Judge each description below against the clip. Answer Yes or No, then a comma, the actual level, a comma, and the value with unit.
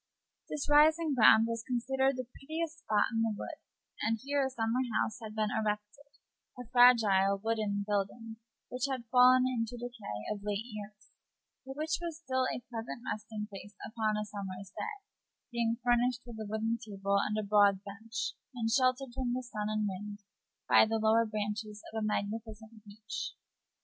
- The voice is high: Yes, high, 225 Hz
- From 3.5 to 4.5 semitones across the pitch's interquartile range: No, average, 3.0 semitones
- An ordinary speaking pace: Yes, average, 170 wpm